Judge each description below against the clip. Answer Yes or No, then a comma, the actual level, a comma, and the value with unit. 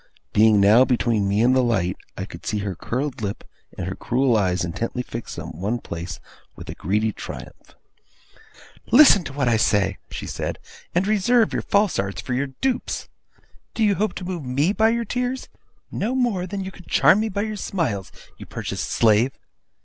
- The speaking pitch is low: Yes, low, 125 Hz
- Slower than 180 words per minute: No, average, 190 wpm